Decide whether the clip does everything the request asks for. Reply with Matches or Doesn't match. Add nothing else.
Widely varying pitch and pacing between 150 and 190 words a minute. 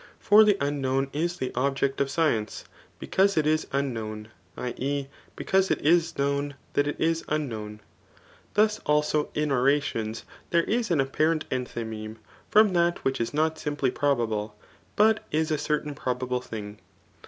Doesn't match